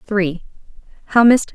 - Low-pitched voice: No, high, 205 Hz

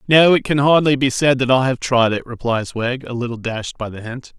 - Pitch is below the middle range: Yes, low, 125 Hz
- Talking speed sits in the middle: No, fast, 260 wpm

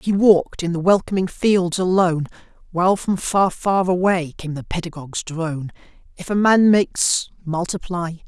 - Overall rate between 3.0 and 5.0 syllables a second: Yes, 4.9 syllables/s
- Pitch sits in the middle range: Yes, medium, 180 Hz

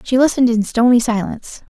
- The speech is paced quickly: No, average, 170 wpm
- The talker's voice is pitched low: No, high, 240 Hz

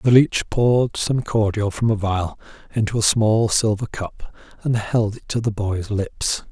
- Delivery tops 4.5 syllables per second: No, 4.2 syllables/s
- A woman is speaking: No, male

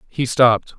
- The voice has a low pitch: Yes, low, 125 Hz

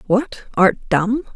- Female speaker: Yes, female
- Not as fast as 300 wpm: Yes, slow, 135 wpm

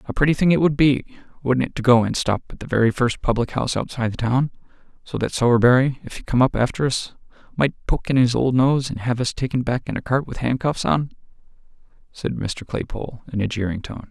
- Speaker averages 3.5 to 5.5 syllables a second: No, 5.9 syllables/s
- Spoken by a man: Yes, male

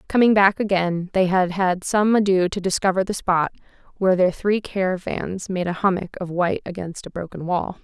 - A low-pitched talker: No, medium, 185 Hz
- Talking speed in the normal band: Yes, average, 190 wpm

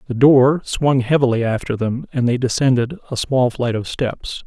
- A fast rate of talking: No, average, 190 wpm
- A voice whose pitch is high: No, low, 125 Hz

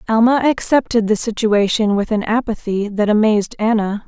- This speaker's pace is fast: No, average, 145 wpm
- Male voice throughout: No, female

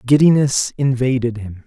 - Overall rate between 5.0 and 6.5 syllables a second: No, 4.7 syllables/s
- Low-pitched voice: Yes, low, 125 Hz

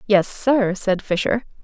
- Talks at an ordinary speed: Yes, average, 145 wpm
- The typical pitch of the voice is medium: No, high, 210 Hz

